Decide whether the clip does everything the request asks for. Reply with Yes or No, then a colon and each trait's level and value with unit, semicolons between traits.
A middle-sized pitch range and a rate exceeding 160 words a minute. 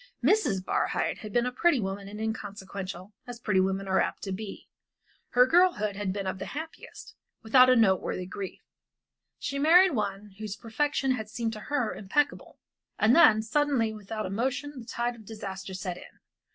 Yes: average, 4.4 semitones; average, 180 wpm